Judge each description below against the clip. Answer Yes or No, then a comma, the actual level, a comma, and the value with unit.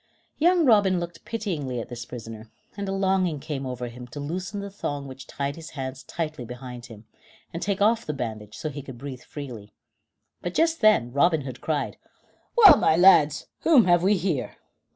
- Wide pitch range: Yes, wide, 7.1 semitones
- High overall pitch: No, medium, 150 Hz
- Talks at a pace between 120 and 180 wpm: No, average, 195 wpm